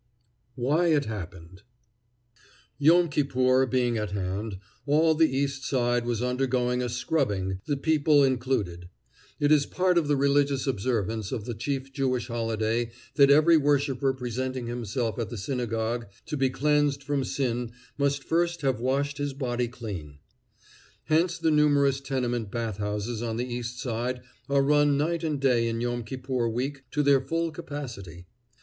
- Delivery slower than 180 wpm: Yes, average, 155 wpm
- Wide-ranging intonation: No, average, 3.4 semitones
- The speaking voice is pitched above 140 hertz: No, low, 130 Hz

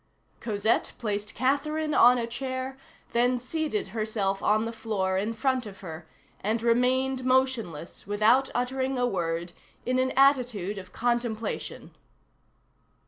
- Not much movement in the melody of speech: No, average, 3.8 semitones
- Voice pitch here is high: Yes, high, 235 Hz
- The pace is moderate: No, slow, 130 wpm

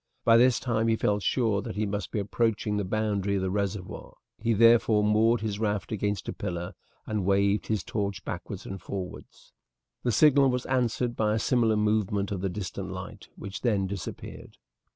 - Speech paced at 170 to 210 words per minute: Yes, average, 185 wpm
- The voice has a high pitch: No, low, 105 Hz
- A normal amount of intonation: No, narrow, 2.3 semitones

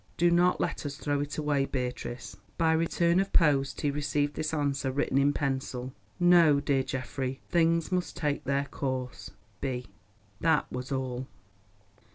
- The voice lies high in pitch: No, medium, 140 Hz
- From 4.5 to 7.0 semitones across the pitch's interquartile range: No, average, 3.4 semitones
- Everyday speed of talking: Yes, average, 150 wpm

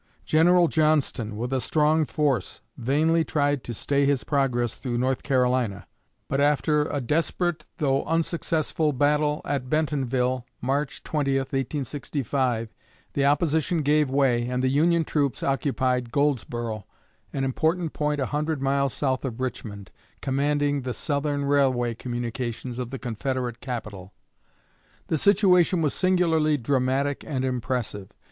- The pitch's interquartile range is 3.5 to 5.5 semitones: No, average, 3.1 semitones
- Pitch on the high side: No, medium, 140 Hz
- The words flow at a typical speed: No, slow, 130 wpm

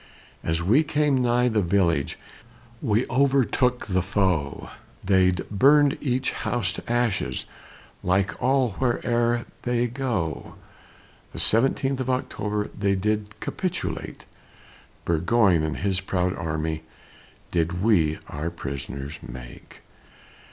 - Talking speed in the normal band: No, slow, 110 wpm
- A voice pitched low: Yes, low, 105 Hz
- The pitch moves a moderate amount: No, wide, 6.2 semitones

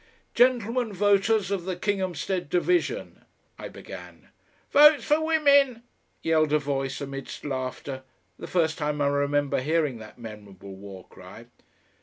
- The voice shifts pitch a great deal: Yes, wide, 8.1 semitones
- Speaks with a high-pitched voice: No, medium, 160 Hz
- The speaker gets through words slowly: Yes, slow, 130 wpm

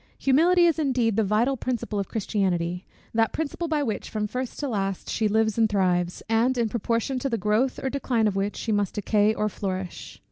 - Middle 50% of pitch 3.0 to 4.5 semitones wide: Yes, average, 4.0 semitones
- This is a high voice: Yes, high, 220 Hz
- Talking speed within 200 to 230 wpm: Yes, fast, 205 wpm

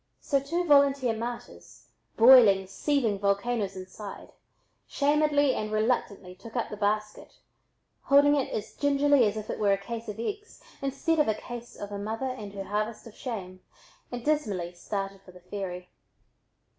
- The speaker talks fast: No, average, 160 wpm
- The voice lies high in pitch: Yes, high, 220 Hz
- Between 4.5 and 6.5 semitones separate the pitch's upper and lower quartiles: Yes, wide, 5.4 semitones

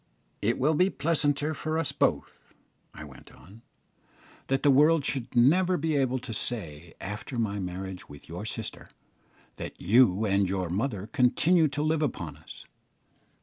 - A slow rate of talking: No, average, 155 wpm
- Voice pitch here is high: No, low, 120 Hz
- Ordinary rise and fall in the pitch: No, wide, 7.4 semitones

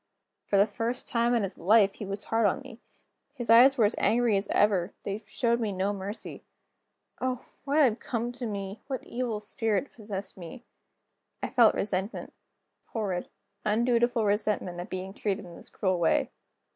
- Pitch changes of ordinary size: Yes, average, 3.2 semitones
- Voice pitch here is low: No, high, 215 Hz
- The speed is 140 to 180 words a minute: Yes, average, 170 wpm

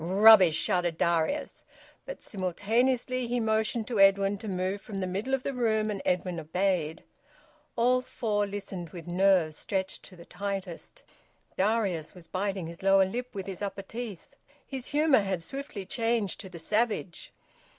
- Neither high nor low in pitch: No, high, 195 Hz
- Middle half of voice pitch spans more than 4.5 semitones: No, average, 3.7 semitones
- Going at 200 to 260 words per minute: No, average, 160 wpm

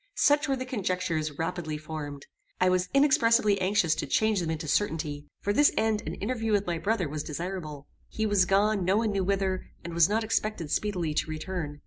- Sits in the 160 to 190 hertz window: Yes, medium, 185 Hz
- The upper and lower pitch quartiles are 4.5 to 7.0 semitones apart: Yes, average, 5.1 semitones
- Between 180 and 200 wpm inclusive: Yes, average, 195 wpm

